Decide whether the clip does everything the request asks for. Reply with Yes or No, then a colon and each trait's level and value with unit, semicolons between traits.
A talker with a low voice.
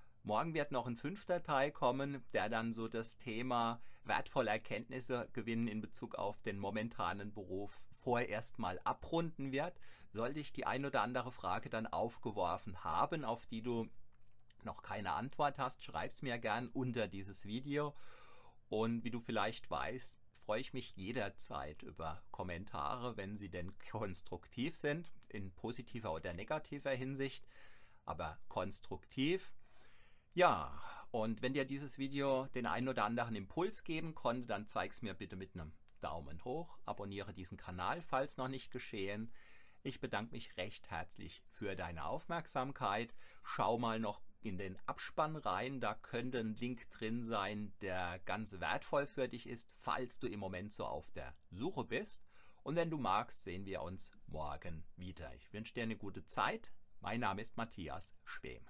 Yes: low, 115 Hz